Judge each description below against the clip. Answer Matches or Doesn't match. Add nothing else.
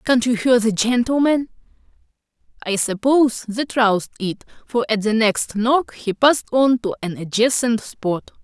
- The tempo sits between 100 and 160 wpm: Matches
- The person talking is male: Doesn't match